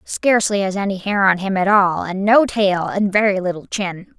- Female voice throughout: Yes, female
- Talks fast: Yes, fast, 215 wpm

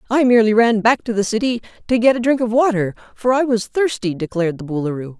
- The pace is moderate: No, fast, 230 wpm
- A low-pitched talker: No, high, 225 Hz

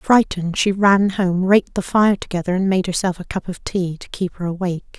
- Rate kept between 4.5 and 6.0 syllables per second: Yes, 5.5 syllables/s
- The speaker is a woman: Yes, female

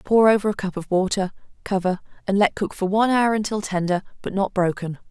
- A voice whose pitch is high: Yes, high, 195 Hz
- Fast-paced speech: Yes, fast, 210 wpm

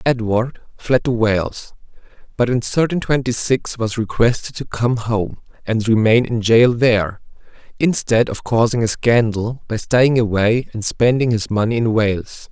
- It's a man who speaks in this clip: Yes, male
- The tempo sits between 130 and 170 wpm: Yes, average, 160 wpm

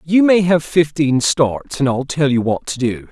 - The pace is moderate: No, fast, 230 wpm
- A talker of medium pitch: Yes, medium, 145 Hz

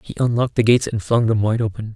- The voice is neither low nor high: No, low, 115 Hz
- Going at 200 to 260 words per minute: No, fast, 275 wpm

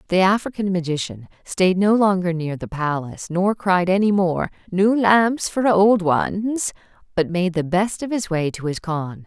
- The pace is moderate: Yes, average, 180 wpm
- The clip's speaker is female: Yes, female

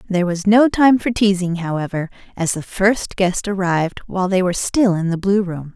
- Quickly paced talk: Yes, fast, 210 wpm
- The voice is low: No, high, 190 Hz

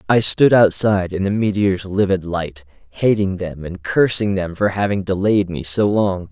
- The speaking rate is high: No, average, 180 wpm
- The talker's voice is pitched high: No, very low, 95 Hz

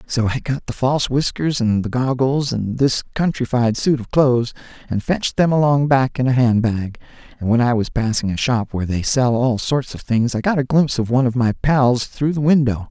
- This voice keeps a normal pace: No, fast, 230 wpm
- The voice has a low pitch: Yes, low, 125 Hz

